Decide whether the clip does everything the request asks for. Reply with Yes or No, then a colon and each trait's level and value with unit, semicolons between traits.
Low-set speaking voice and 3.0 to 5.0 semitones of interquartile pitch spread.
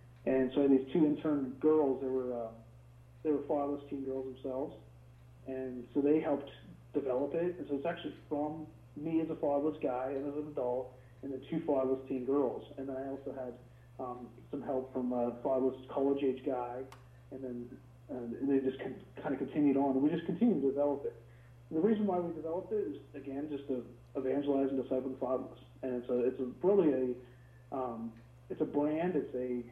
No: low, 130 Hz; narrow, 2.6 semitones